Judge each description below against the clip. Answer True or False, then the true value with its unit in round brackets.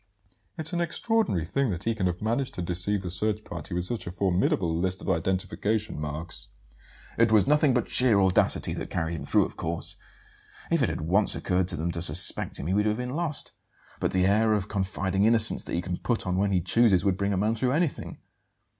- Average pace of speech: False (220 wpm)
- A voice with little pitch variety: False (4.4 semitones)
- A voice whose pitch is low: True (100 Hz)